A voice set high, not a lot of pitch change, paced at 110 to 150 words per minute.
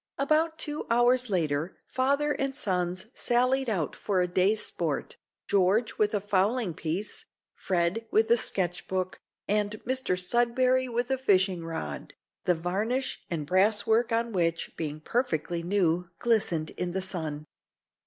No: high, 200 Hz; wide, 5.4 semitones; average, 145 wpm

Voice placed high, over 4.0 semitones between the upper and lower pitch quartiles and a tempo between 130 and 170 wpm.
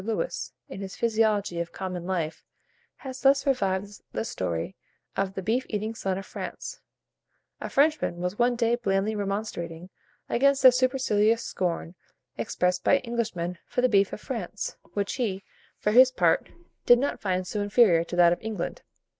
Yes: high, 205 Hz; average, 4.6 semitones; average, 165 wpm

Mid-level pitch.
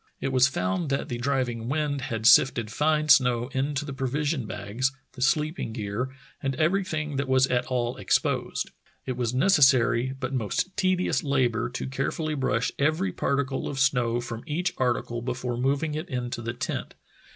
No: low, 130 Hz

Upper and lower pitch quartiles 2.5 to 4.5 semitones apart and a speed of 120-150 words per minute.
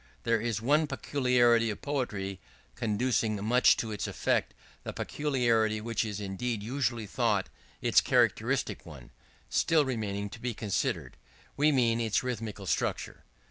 Yes: average, 3.0 semitones; average, 140 wpm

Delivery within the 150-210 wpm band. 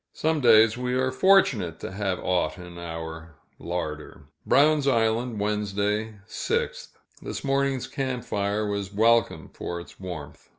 No: slow, 135 wpm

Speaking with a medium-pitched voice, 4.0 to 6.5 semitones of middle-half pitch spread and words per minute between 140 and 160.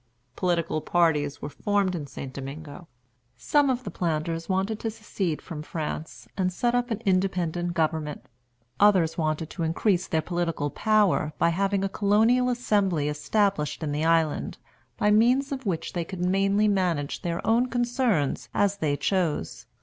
Yes: medium, 180 Hz; average, 4.7 semitones; average, 155 wpm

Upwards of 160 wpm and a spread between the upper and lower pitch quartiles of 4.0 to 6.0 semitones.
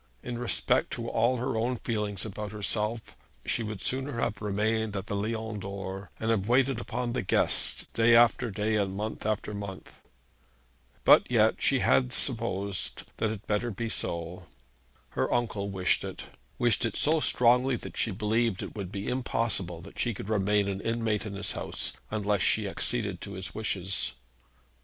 No: average, 175 wpm; average, 2.8 semitones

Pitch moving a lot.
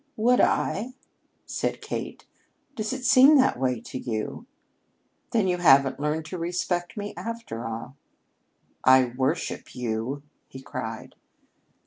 Yes: wide, 8.9 semitones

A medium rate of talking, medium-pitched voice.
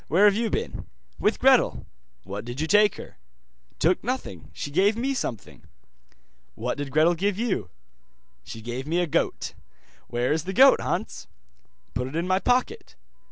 Yes: average, 165 wpm; medium, 170 Hz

